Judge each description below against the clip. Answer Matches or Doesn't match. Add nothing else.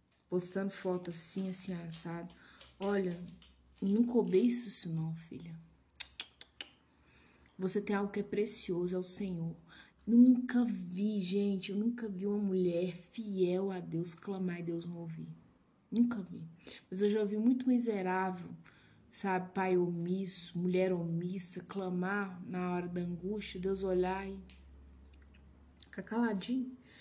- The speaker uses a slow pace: Doesn't match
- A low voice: Doesn't match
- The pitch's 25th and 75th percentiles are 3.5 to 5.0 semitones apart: Doesn't match